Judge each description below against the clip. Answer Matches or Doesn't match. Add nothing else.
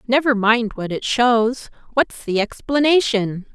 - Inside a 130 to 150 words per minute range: Matches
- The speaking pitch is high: Matches